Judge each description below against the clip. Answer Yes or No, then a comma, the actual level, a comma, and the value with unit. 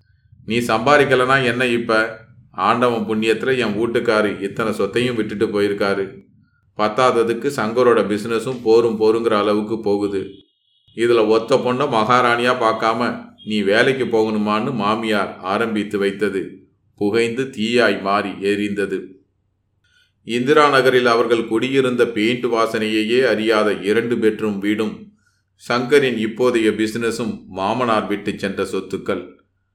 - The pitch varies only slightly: Yes, narrow, 2.3 semitones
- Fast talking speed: No, average, 105 wpm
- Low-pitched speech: Yes, low, 110 Hz